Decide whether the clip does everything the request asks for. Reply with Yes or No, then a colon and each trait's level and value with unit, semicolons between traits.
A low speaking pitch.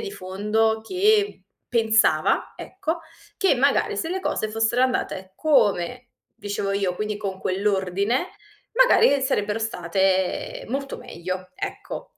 No: high, 220 Hz